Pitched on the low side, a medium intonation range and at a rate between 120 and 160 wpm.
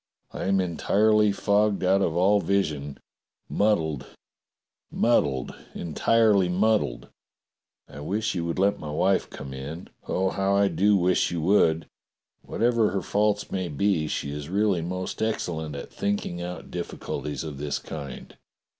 Yes: very low, 95 Hz; average, 4.5 semitones; average, 145 wpm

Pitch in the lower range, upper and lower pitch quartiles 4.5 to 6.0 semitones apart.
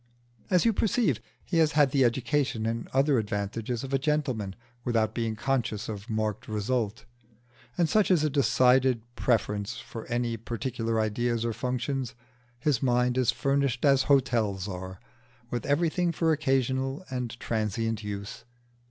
No: low, 120 Hz; average, 3.6 semitones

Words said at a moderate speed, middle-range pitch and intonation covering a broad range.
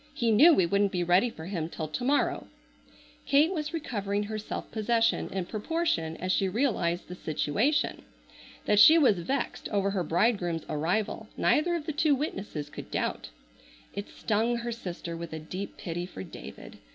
No: average, 175 wpm; high, 205 Hz; wide, 5.9 semitones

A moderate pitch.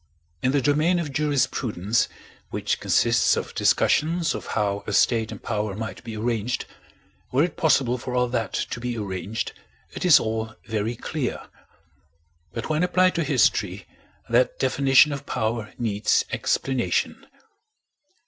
No: low, 120 Hz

